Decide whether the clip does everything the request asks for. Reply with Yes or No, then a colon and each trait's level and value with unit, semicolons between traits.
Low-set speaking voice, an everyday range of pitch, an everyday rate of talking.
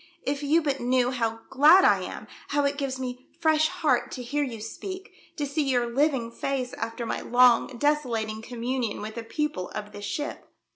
No: very high, 255 Hz; average, 3.9 semitones; average, 190 wpm